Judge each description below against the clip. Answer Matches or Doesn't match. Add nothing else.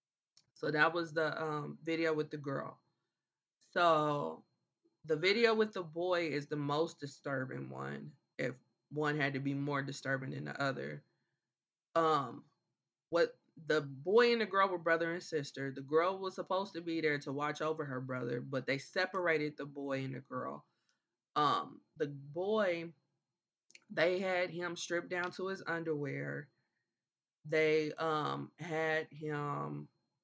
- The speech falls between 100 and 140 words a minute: Doesn't match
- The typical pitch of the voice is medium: Matches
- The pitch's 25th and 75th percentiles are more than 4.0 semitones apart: Doesn't match